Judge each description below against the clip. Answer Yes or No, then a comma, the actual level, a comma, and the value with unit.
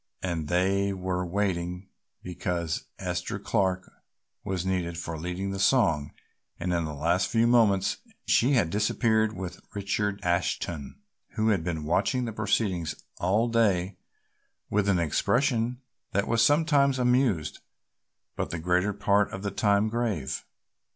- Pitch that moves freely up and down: No, average, 3.8 semitones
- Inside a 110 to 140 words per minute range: Yes, slow, 135 wpm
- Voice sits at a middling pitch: No, very low, 95 Hz